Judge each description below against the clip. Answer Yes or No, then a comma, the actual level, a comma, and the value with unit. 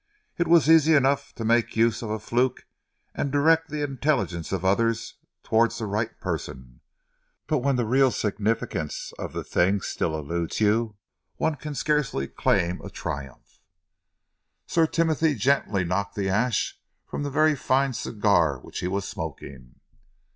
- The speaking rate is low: No, average, 155 wpm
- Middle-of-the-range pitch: No, low, 115 Hz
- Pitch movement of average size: No, wide, 6.8 semitones